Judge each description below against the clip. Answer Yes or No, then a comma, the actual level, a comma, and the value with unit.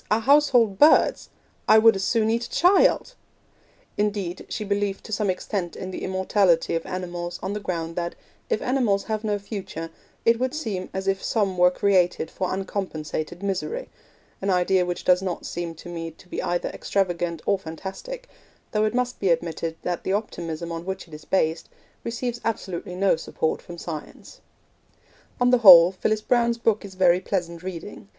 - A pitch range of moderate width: Yes, average, 3.8 semitones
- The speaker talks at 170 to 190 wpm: Yes, average, 180 wpm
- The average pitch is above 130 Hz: Yes, high, 190 Hz